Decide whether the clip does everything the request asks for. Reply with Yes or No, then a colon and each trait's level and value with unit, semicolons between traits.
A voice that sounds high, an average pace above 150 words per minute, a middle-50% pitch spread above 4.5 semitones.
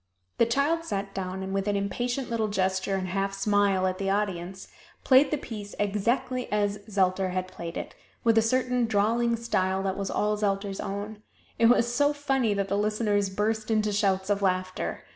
No: high, 205 Hz; average, 185 wpm; average, 3.1 semitones